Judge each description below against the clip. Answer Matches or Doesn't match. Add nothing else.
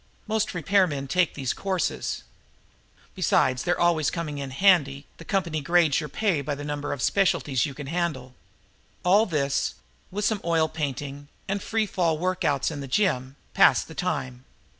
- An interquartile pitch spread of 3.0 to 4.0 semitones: Doesn't match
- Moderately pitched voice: Matches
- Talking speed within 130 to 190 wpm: Matches